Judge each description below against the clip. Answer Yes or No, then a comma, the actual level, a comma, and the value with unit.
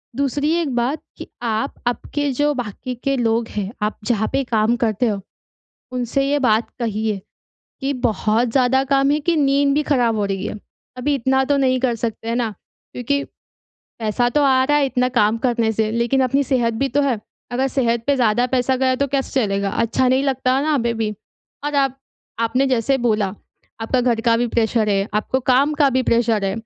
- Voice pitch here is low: No, very high, 250 Hz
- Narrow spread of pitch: No, average, 3.3 semitones